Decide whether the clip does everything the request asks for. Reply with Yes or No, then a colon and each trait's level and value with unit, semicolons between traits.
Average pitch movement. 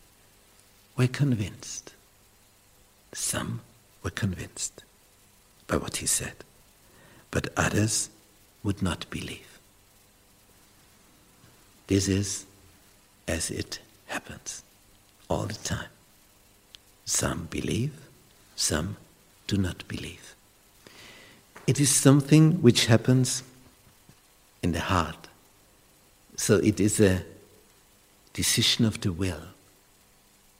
No: narrow, 1.5 semitones